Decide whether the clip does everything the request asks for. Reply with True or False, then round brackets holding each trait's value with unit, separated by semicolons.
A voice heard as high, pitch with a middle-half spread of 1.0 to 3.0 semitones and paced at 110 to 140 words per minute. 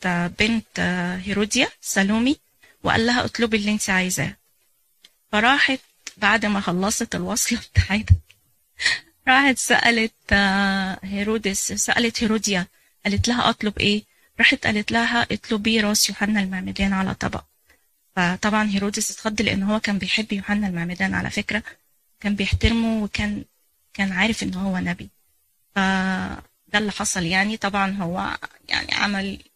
True (205 Hz; 2.6 semitones; 120 wpm)